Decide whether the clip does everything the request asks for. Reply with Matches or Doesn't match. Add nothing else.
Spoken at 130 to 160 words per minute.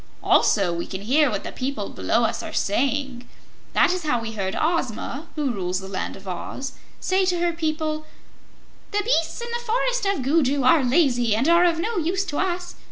Doesn't match